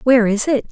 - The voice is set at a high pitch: Yes, high, 240 Hz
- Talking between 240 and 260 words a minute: Yes, fast, 255 wpm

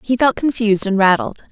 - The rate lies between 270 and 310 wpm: No, average, 200 wpm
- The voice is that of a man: No, female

